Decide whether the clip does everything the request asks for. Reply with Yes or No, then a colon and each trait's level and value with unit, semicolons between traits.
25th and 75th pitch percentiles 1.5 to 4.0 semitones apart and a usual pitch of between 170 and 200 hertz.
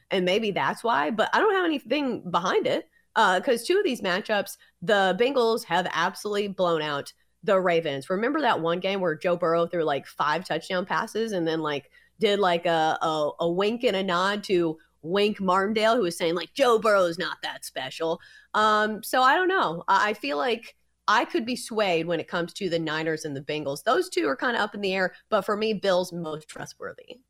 No: average, 4.5 semitones; high, 190 Hz